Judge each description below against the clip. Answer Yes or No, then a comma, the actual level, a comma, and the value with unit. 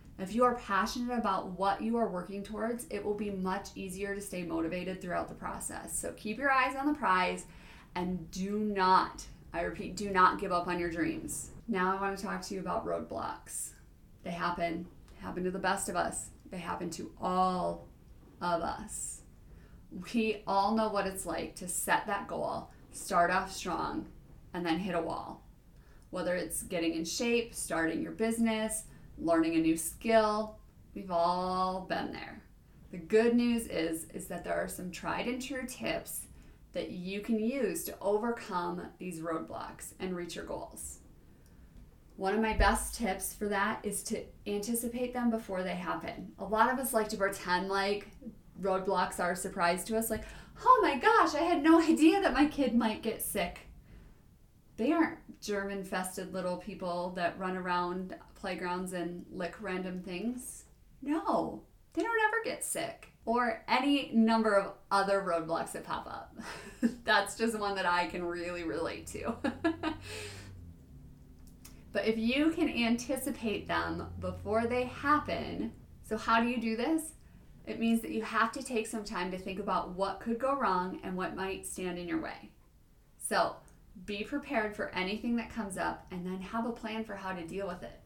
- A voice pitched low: No, high, 195 Hz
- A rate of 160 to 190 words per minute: Yes, average, 175 wpm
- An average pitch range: Yes, average, 4.3 semitones